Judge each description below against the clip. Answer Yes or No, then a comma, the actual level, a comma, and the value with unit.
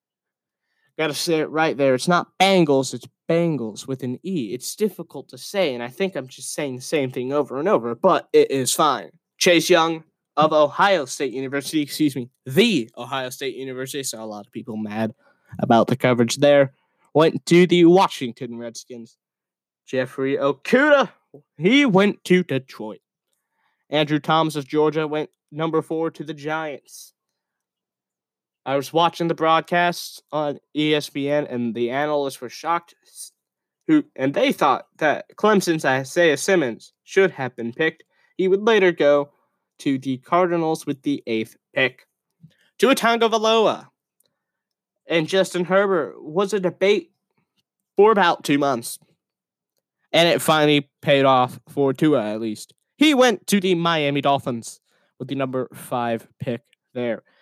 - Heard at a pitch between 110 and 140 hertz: No, medium, 150 Hz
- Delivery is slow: No, average, 150 wpm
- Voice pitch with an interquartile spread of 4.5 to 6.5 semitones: Yes, average, 4.9 semitones